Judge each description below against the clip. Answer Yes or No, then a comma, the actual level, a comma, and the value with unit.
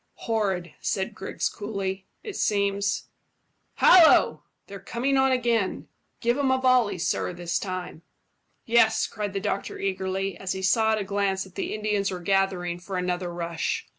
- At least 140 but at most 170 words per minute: Yes, average, 160 wpm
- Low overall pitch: No, high, 195 Hz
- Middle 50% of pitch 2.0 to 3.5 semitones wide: Yes, average, 2.8 semitones